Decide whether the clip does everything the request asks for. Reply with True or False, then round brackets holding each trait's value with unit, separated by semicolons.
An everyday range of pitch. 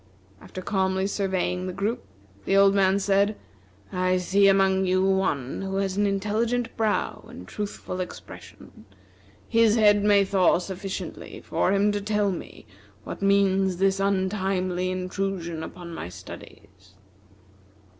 False (1.5 semitones)